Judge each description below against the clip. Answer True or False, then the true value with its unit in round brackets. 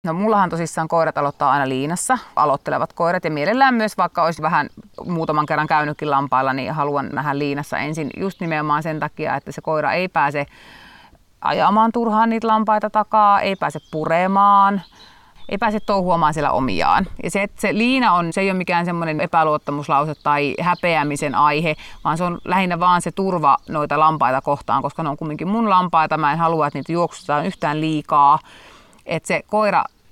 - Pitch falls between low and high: True (165 Hz)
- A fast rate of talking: True (175 wpm)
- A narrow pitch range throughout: False (4.6 semitones)